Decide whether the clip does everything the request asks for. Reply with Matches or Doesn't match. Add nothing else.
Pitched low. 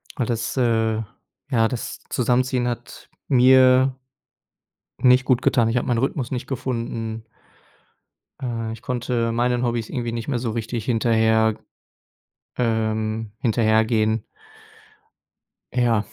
Matches